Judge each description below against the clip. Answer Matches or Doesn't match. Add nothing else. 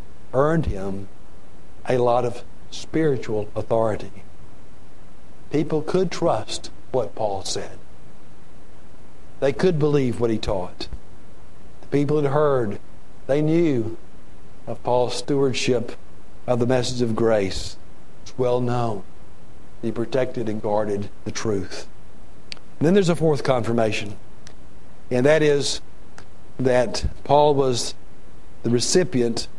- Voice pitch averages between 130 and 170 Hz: Doesn't match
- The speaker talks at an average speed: Doesn't match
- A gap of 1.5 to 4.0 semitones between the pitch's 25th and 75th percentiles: Doesn't match